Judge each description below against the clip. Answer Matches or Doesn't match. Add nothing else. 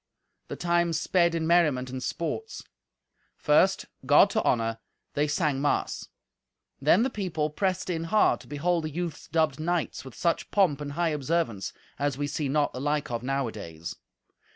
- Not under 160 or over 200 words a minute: Matches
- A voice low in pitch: Doesn't match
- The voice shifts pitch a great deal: Doesn't match